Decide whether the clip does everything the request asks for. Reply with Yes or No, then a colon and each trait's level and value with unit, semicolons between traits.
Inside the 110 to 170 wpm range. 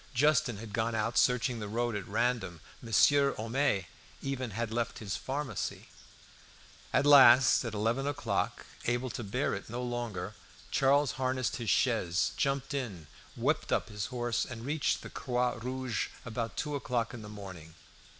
Yes: average, 160 wpm